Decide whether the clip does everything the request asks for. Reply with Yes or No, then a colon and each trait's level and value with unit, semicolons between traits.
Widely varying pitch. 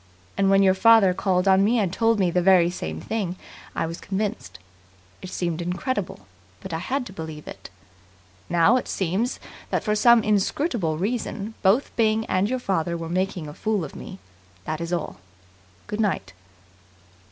No: average, 4.1 semitones